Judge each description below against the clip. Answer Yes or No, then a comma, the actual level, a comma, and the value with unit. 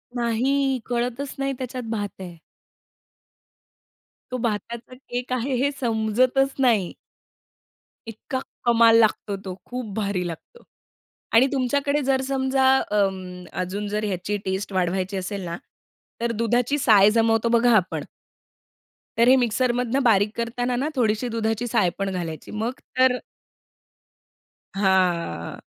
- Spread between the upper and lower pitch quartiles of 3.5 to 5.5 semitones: Yes, average, 4.1 semitones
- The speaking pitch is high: Yes, high, 230 Hz